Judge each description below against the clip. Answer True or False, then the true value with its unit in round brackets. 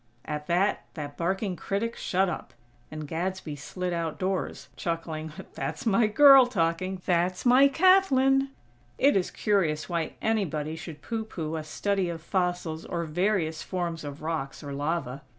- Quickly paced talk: False (150 wpm)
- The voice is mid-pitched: True (175 Hz)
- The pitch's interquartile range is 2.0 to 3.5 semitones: False (4.3 semitones)